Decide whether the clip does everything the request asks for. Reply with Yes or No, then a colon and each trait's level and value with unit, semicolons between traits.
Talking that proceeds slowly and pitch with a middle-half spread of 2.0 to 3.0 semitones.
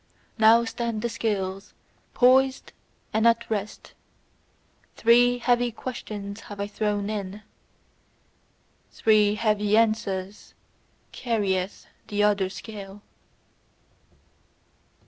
Yes: slow, 90 wpm; narrow, 2.4 semitones